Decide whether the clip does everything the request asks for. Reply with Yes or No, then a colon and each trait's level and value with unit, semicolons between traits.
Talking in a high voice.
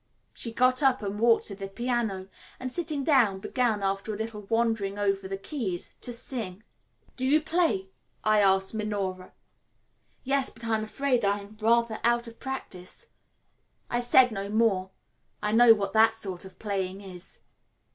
Yes: high, 220 Hz